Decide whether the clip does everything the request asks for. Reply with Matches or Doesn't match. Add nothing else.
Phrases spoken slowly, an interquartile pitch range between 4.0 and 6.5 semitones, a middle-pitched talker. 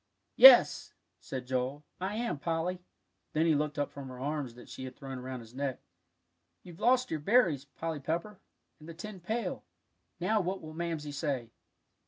Doesn't match